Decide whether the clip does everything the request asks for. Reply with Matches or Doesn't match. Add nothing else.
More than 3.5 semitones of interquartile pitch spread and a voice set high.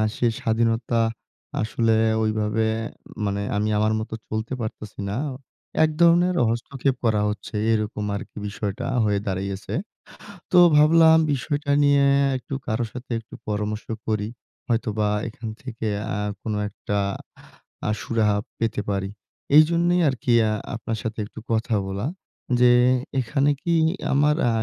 Doesn't match